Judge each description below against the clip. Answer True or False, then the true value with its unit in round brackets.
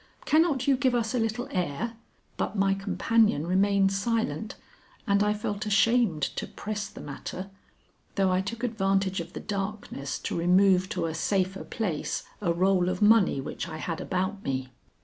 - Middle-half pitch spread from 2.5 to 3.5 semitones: True (3.2 semitones)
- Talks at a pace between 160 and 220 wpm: True (170 wpm)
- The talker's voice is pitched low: False (195 Hz)